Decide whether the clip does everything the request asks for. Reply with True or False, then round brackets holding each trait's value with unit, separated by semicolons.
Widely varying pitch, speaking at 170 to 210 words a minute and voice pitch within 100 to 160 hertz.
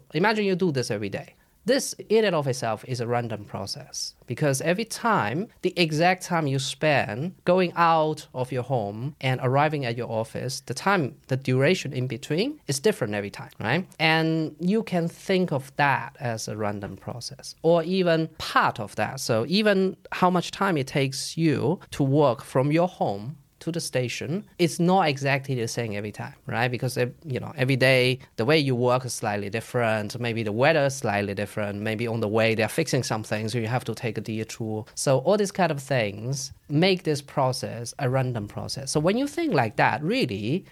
True (5.7 semitones; 200 wpm; 135 Hz)